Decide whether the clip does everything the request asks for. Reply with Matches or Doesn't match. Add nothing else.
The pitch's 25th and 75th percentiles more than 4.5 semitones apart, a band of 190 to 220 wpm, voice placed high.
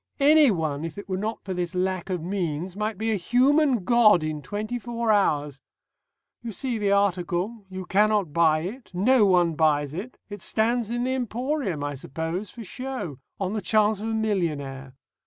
Doesn't match